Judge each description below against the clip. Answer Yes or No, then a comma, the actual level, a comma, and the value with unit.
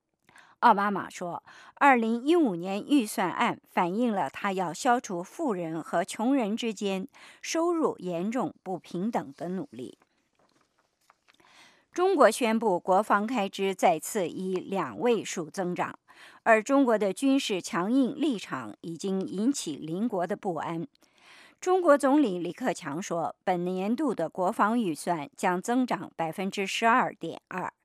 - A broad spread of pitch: Yes, wide, 5.9 semitones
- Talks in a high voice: Yes, high, 205 Hz